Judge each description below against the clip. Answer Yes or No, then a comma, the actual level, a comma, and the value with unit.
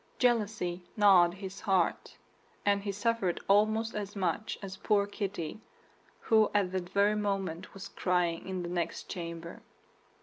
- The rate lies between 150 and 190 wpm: No, average, 140 wpm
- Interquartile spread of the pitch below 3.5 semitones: Yes, average, 2.7 semitones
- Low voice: No, high, 195 Hz